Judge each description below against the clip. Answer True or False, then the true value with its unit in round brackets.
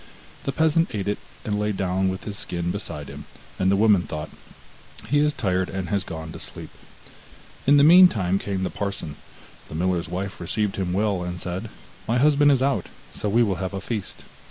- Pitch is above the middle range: False (100 Hz)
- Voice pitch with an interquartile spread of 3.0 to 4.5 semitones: True (4.1 semitones)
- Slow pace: False (200 wpm)